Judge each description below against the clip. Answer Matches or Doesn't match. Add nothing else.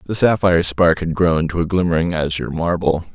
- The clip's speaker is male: Matches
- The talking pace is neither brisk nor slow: Matches